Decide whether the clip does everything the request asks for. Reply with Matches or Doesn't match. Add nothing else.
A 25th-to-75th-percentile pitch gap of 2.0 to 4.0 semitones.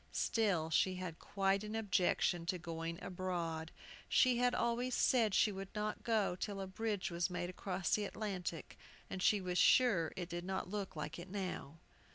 Matches